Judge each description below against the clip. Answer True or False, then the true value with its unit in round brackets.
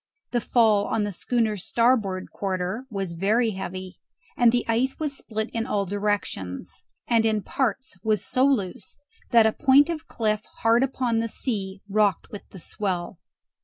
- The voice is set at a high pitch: True (220 Hz)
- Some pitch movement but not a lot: True (3.5 semitones)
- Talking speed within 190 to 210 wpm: False (165 wpm)